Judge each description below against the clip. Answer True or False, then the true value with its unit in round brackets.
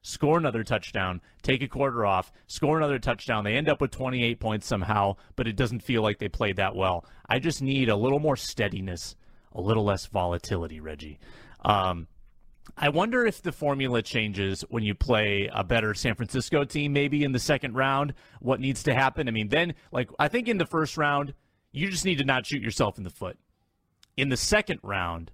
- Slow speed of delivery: False (205 wpm)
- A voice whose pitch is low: True (120 Hz)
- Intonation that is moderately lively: False (6.0 semitones)